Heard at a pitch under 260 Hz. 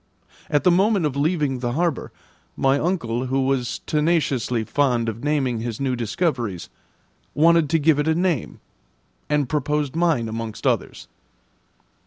Yes: medium, 140 Hz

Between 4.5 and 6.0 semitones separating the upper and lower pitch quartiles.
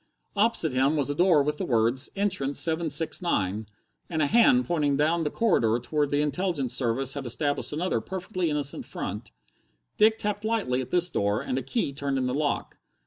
Yes: average, 5.0 semitones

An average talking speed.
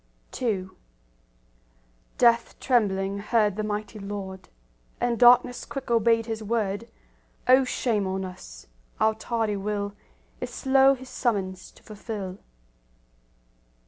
No: slow, 110 wpm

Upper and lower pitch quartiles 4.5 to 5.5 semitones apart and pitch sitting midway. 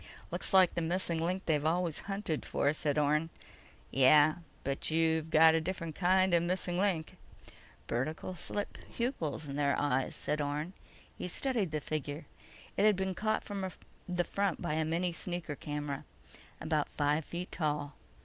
No: average, 3.5 semitones; medium, 160 Hz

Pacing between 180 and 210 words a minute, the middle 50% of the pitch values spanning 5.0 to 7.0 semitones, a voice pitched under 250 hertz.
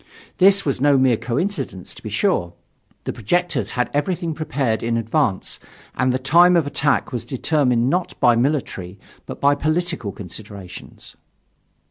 No: average, 145 wpm; wide, 5.6 semitones; low, 135 Hz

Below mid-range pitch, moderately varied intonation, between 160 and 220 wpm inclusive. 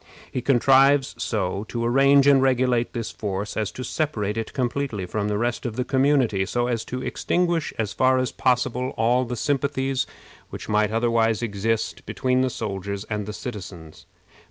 Yes: low, 120 Hz; average, 3.6 semitones; average, 170 wpm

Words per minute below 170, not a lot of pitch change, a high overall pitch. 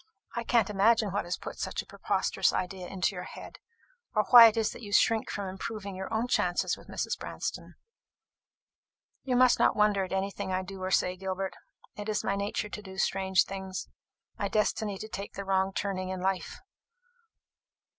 No: average, 190 wpm; narrow, 1.9 semitones; high, 195 Hz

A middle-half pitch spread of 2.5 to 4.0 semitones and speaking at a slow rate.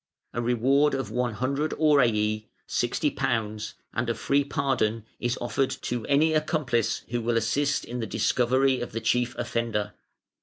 No: average, 3.4 semitones; average, 145 wpm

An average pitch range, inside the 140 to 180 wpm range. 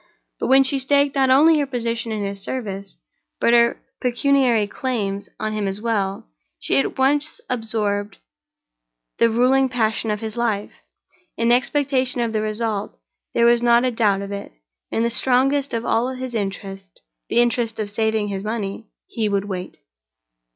Yes: average, 3.7 semitones; average, 160 wpm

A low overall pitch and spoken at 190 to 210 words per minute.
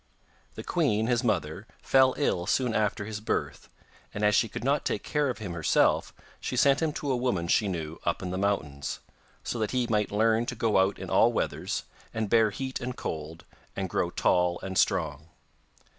Yes: low, 105 Hz; average, 200 wpm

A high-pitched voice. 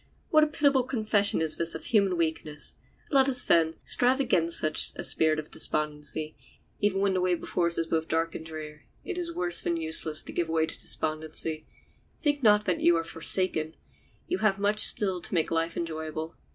No: medium, 170 Hz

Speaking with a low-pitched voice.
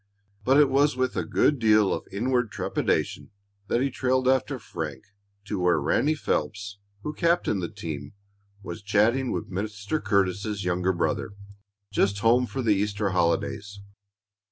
Yes: low, 105 Hz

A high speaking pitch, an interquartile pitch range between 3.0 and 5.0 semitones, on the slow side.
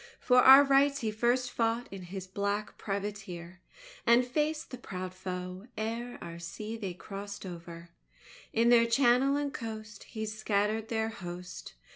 No: high, 215 Hz; average, 4.5 semitones; average, 150 wpm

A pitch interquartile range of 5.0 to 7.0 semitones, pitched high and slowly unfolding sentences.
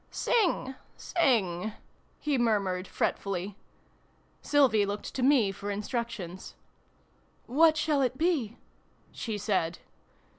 Yes: wide, 5.6 semitones; high, 225 Hz; slow, 125 wpm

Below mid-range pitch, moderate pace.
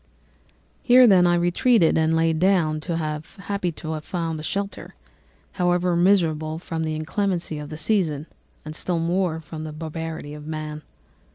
No: medium, 165 Hz; average, 155 wpm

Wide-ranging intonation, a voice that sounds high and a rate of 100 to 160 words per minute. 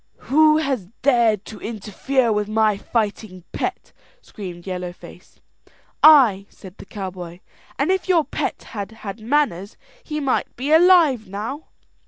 Yes: wide, 6.3 semitones; high, 220 Hz; average, 140 wpm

